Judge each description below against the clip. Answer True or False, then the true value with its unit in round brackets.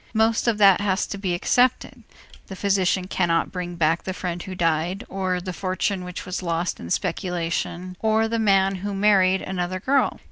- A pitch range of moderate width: False (2.1 semitones)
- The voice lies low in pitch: False (185 Hz)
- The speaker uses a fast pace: False (180 wpm)